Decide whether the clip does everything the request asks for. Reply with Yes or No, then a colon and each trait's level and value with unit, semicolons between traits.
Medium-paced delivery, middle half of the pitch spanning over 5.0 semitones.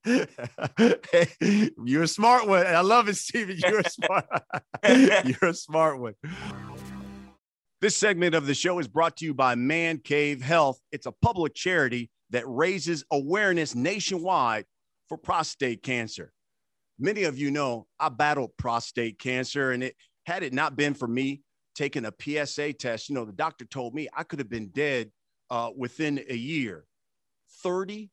Yes: average, 160 wpm; wide, 5.5 semitones